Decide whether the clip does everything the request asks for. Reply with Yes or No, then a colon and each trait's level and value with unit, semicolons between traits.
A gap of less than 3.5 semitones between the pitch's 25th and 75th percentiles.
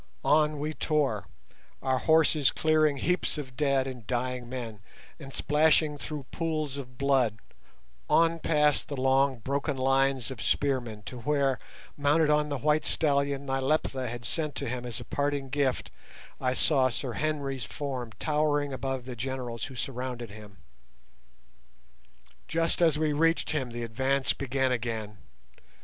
Yes: average, 2.9 semitones